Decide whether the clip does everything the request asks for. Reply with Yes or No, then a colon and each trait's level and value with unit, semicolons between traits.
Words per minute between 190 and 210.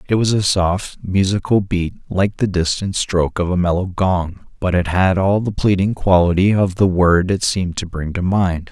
Yes: fast, 205 wpm